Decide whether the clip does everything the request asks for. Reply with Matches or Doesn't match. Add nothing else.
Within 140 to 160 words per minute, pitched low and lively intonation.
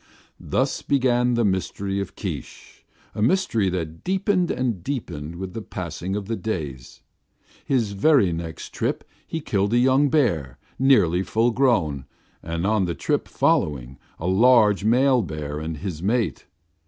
Matches